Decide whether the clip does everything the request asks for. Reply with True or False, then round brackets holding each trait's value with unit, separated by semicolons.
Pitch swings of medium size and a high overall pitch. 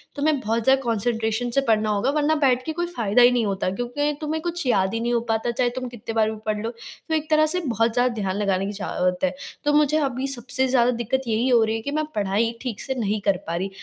True (3.8 semitones; 235 Hz)